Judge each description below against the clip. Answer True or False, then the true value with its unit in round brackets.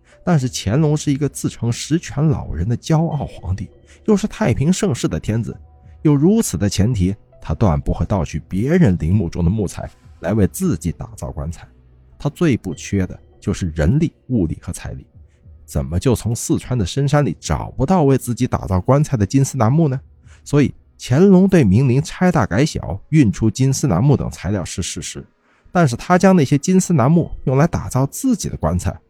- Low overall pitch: True (120 Hz)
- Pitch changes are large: True (8.6 semitones)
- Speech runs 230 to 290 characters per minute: True (285 characters per minute)